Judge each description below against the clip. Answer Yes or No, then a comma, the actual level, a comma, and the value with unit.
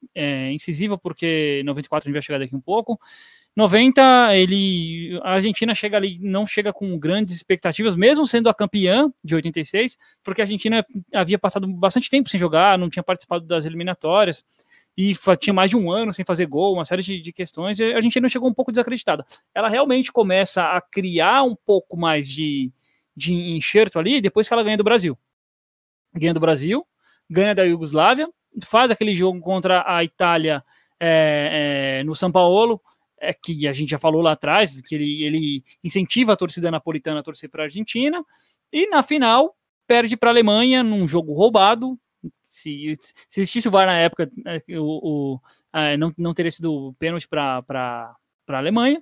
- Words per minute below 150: No, average, 180 wpm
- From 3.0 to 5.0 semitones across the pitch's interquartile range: No, wide, 5.6 semitones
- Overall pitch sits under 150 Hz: No, medium, 185 Hz